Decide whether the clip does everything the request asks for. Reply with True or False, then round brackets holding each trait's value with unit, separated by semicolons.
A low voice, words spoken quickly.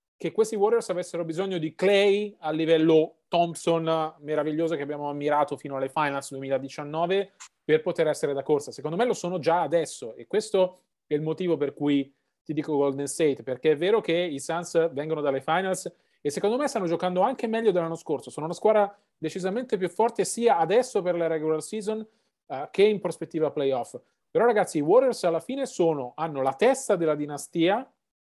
False (165 Hz; 185 wpm)